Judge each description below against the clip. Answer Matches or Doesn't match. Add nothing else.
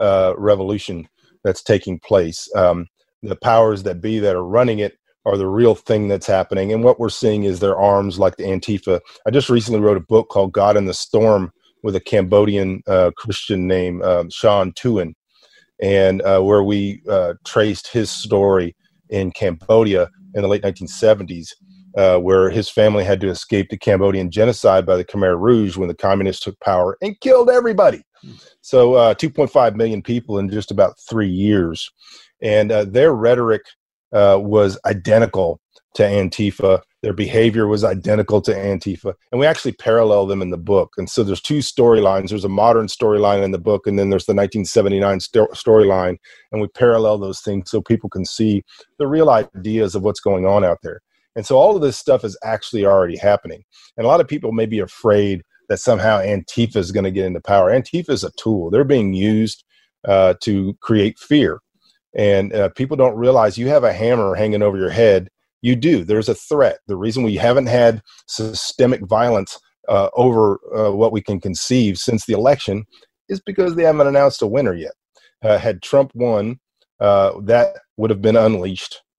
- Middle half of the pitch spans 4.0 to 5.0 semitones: Doesn't match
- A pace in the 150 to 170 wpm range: Doesn't match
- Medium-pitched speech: Doesn't match